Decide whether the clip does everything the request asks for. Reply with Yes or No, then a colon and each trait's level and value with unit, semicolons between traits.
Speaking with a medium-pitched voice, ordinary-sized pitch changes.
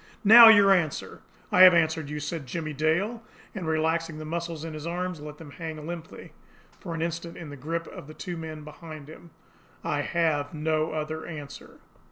No: medium, 160 Hz; narrow, 1.9 semitones